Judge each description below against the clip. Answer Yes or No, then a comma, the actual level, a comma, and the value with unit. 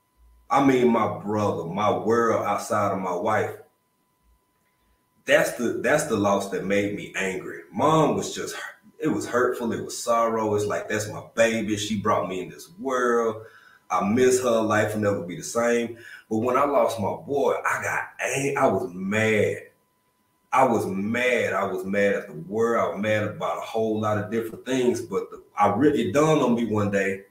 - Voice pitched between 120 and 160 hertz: No, low, 110 Hz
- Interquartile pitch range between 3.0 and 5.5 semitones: No, narrow, 2.4 semitones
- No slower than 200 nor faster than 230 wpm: No, average, 190 wpm